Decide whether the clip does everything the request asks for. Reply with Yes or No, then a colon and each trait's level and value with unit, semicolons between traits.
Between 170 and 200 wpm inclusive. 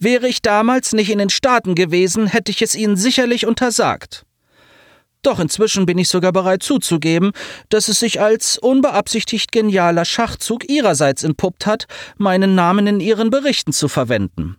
No: average, 155 wpm